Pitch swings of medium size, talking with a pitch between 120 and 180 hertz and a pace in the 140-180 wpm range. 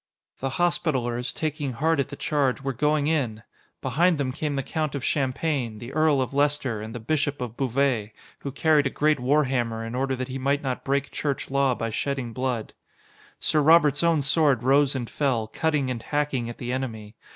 No: average, 3.1 semitones; low, 135 Hz; average, 195 wpm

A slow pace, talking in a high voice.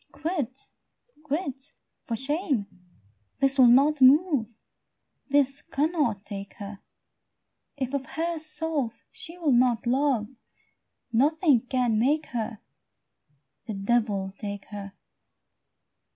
Yes: slow, 100 wpm; very high, 265 Hz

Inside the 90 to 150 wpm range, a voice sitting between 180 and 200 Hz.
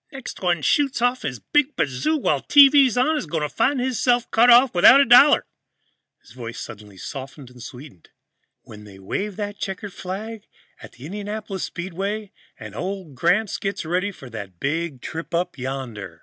No: average, 175 wpm; medium, 185 Hz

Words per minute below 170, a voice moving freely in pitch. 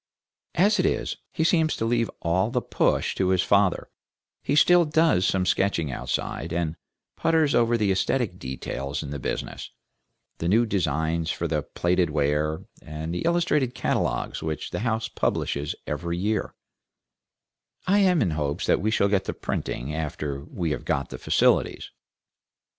Yes: average, 160 wpm; wide, 7.3 semitones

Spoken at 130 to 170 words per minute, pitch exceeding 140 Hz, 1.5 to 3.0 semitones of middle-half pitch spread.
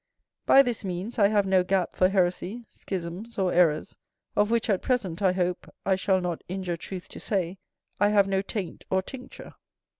No: average, 185 wpm; high, 190 Hz; narrow, 2.4 semitones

